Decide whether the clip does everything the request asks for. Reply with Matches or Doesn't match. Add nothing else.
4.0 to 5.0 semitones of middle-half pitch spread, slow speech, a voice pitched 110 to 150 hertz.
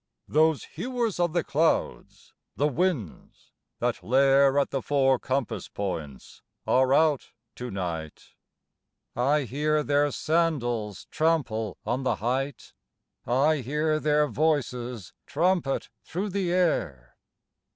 Matches